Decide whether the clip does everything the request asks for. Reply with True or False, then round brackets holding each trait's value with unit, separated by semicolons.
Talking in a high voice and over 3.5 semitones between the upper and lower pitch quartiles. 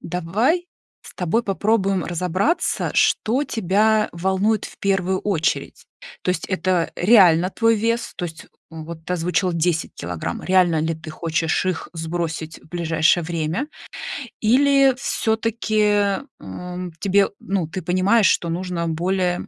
False (180 Hz; 3.9 semitones)